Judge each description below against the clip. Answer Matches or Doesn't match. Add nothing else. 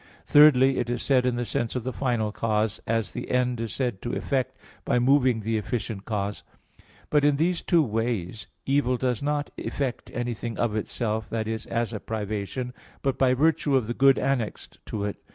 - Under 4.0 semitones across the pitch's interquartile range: Matches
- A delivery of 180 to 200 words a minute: Matches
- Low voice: Matches